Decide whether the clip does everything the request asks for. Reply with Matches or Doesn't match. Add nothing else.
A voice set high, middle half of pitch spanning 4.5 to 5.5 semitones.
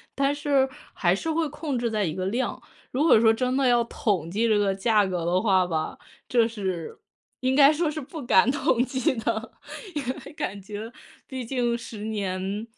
Matches